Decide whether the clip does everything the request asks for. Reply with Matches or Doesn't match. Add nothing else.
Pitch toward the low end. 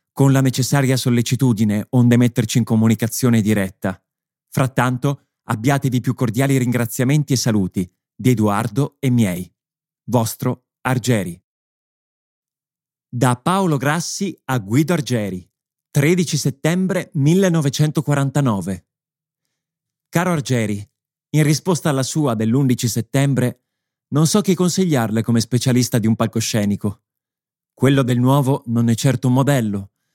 Matches